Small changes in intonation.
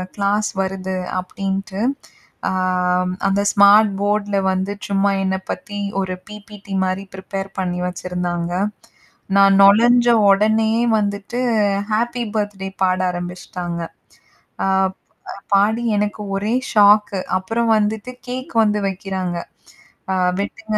Yes: narrow, 2.0 semitones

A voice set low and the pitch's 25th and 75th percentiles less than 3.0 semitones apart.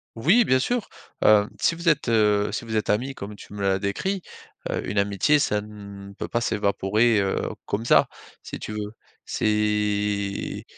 Yes: low, 105 Hz; narrow, 2.6 semitones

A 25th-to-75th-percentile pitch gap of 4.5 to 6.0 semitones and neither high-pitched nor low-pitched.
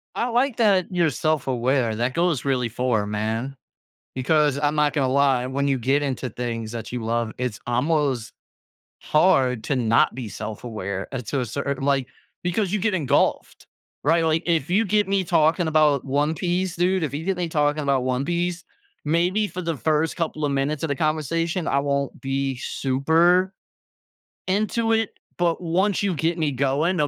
Yes: average, 4.9 semitones; medium, 145 Hz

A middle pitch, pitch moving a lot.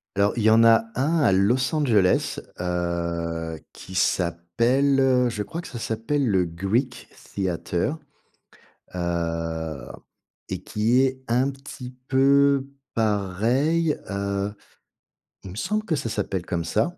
No: low, 110 Hz; wide, 6.9 semitones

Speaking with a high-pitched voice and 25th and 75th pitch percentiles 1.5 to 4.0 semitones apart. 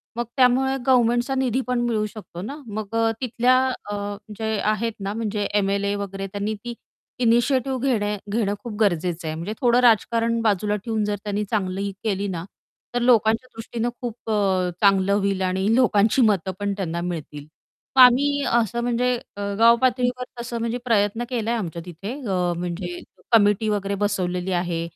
Yes: high, 215 Hz; average, 3.4 semitones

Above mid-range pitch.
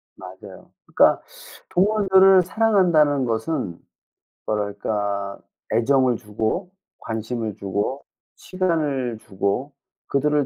No: low, 130 Hz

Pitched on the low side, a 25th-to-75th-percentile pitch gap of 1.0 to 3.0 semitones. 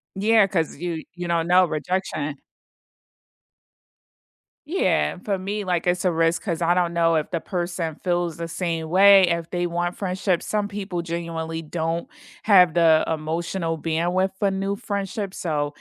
No: medium, 175 Hz; narrow, 2.4 semitones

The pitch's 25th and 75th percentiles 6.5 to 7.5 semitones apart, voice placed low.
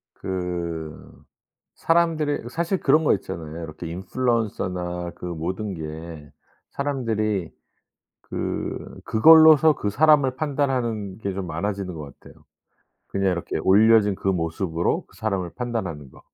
Yes: wide, 6.9 semitones; low, 100 Hz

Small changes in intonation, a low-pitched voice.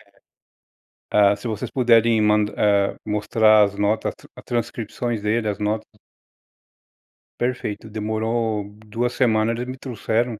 Yes: narrow, 1.9 semitones; low, 110 Hz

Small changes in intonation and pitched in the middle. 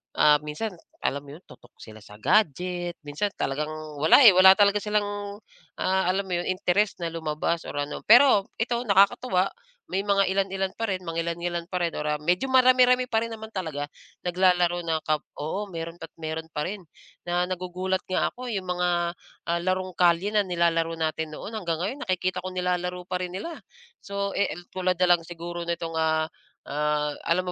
No: average, 3.2 semitones; medium, 180 Hz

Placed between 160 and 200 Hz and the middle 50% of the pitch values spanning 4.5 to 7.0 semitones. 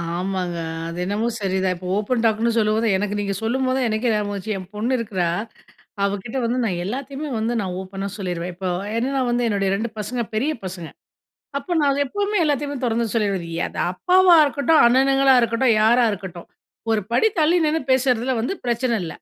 No: high, 225 Hz; average, 5.0 semitones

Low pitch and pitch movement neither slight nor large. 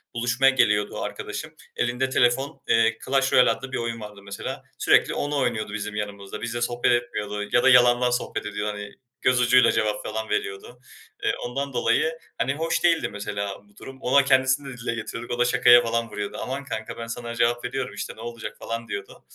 Yes: low, 120 Hz; average, 3.4 semitones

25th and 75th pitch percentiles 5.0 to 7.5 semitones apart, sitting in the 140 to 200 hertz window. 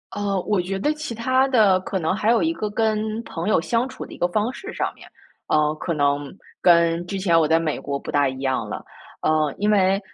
Yes: average, 5.3 semitones; high, 190 Hz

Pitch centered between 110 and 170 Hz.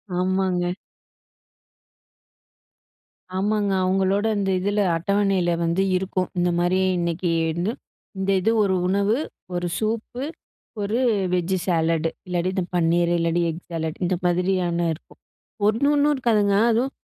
No: medium, 185 Hz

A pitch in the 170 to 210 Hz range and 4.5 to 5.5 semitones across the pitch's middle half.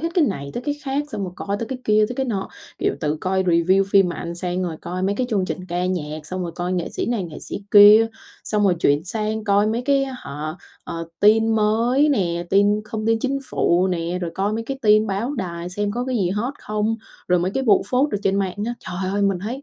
No: high, 200 Hz; average, 3.9 semitones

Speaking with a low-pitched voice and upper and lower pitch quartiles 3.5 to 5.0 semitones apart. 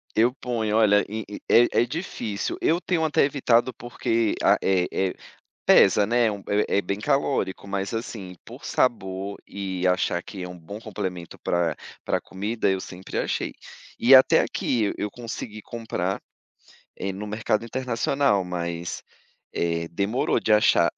Yes: low, 105 Hz; average, 3.9 semitones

